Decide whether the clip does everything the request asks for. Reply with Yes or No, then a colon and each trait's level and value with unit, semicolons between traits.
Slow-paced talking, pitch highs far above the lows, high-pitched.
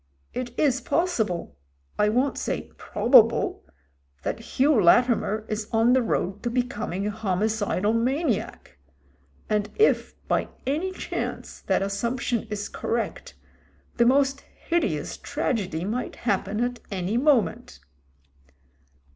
No: slow, 130 wpm; average, 4.3 semitones; high, 225 Hz